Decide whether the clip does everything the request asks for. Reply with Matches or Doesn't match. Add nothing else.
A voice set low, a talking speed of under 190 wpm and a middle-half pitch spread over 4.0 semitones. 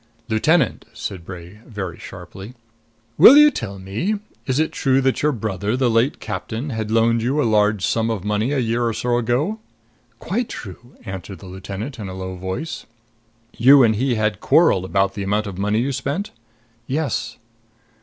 Matches